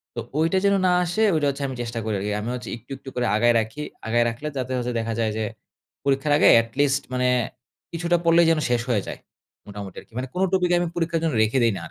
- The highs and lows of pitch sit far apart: Yes, wide, 6.0 semitones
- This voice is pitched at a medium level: No, low, 130 Hz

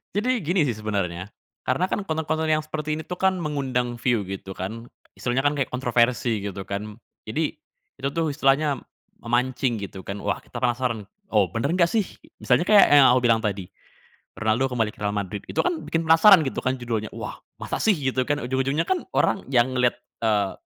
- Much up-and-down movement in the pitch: Yes, wide, 6.1 semitones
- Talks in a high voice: No, low, 130 Hz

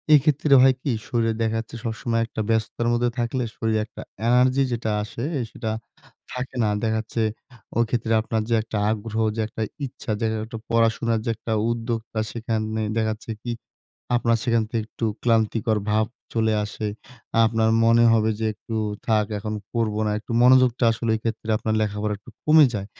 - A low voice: Yes, low, 115 Hz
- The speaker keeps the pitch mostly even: Yes, narrow, 1.3 semitones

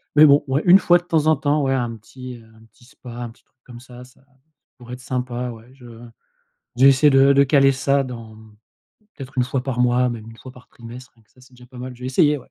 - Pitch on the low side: Yes, low, 125 Hz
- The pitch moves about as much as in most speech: No, narrow, 2.1 semitones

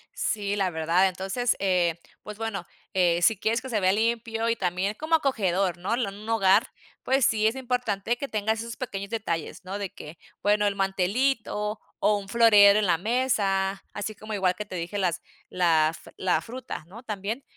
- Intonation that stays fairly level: No, average, 3.2 semitones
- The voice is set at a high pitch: Yes, high, 205 Hz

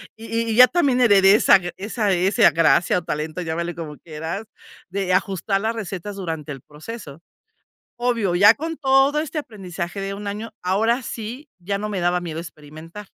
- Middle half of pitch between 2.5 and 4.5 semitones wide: No, average, 4.9 semitones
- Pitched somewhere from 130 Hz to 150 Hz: No, high, 195 Hz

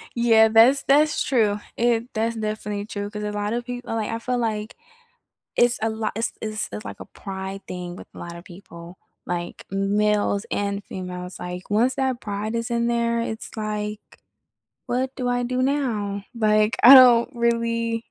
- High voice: Yes, high, 220 Hz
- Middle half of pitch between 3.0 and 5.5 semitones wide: No, narrow, 2.5 semitones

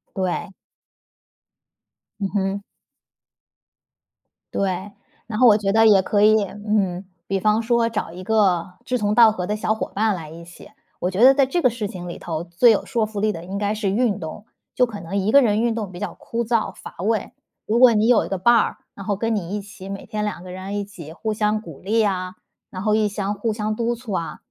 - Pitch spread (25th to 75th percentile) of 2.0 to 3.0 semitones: Yes, average, 2.7 semitones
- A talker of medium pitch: No, high, 205 Hz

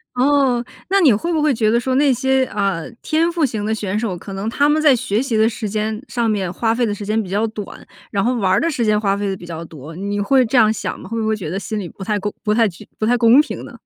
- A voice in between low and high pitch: No, high, 220 Hz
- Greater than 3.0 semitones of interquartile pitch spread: Yes, average, 3.8 semitones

